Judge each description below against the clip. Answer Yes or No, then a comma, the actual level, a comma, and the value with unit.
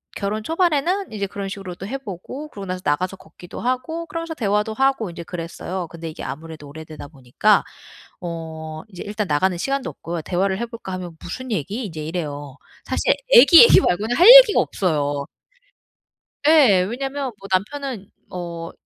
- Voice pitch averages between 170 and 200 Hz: Yes, high, 195 Hz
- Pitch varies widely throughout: Yes, wide, 7.4 semitones